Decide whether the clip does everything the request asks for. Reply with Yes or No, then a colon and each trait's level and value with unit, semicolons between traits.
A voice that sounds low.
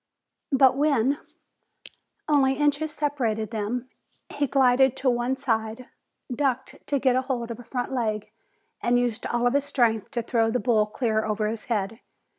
No: high, 245 Hz